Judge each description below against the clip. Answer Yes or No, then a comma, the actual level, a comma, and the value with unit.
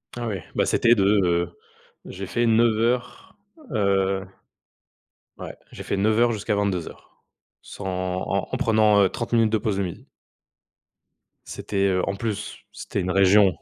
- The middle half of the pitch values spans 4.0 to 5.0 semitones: No, average, 2.8 semitones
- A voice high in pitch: No, low, 105 Hz